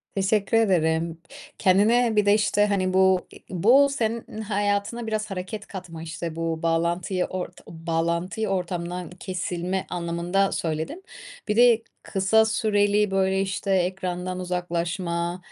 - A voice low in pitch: No, medium, 185 Hz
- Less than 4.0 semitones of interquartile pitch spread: Yes, average, 3.3 semitones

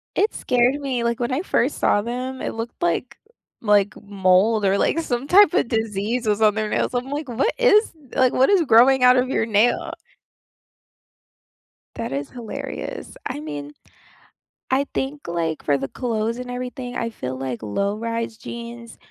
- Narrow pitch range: No, average, 3.8 semitones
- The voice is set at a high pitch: Yes, high, 235 Hz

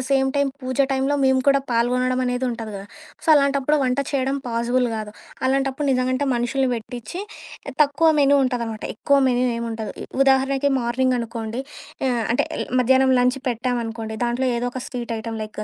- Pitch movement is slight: Yes, narrow, 2.3 semitones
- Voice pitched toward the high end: Yes, very high, 255 Hz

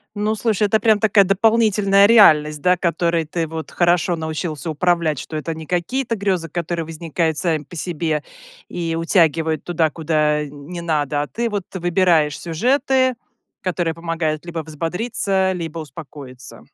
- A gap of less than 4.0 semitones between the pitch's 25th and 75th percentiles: Yes, average, 3.3 semitones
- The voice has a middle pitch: Yes, medium, 170 Hz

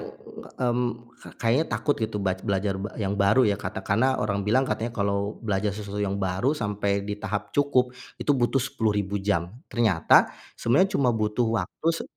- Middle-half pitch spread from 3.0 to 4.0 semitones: Yes, average, 3.6 semitones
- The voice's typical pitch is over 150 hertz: No, low, 105 Hz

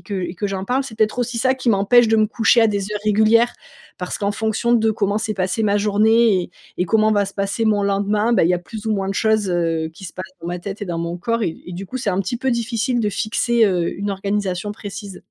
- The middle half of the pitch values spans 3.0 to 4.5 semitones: No, narrow, 2.6 semitones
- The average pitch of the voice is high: Yes, high, 205 Hz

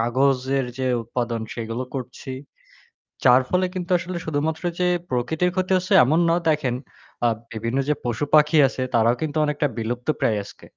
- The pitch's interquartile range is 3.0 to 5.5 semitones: Yes, average, 4.7 semitones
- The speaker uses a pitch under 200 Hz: Yes, low, 135 Hz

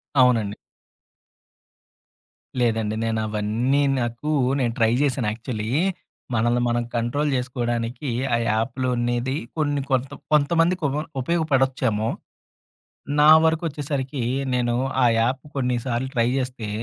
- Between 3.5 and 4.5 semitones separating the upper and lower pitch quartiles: No, average, 2.9 semitones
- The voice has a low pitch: Yes, low, 125 Hz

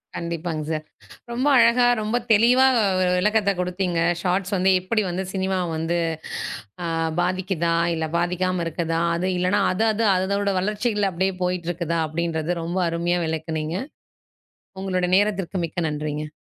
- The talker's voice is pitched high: No, medium, 180 Hz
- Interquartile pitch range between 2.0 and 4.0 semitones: Yes, average, 2.8 semitones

